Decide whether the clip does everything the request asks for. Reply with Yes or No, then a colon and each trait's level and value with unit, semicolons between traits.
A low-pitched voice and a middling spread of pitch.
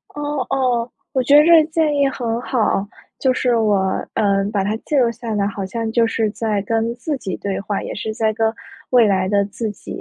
No: high, 225 Hz; average, 3.8 semitones